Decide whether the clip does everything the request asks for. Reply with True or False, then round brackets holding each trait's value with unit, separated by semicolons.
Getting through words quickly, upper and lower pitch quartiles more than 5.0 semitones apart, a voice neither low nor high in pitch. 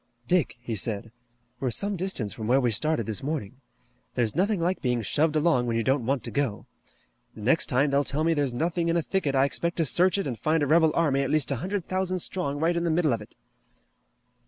True (235 wpm; 5.5 semitones; 145 Hz)